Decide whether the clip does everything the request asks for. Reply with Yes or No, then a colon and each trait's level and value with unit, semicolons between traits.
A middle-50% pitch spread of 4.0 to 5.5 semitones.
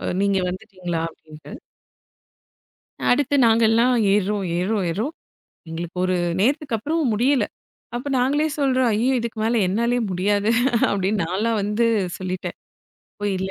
Yes: average, 4.3 semitones